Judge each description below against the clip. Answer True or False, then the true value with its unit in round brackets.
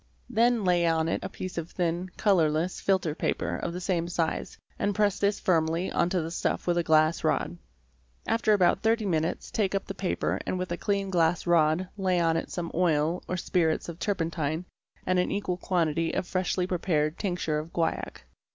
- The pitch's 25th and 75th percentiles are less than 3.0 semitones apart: True (2.4 semitones)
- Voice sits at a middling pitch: True (175 Hz)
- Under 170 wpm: False (195 wpm)